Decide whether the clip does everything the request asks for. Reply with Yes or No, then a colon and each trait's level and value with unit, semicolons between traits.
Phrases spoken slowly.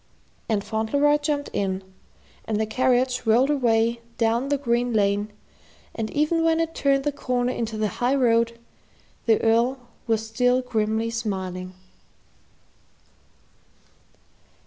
Yes: slow, 125 wpm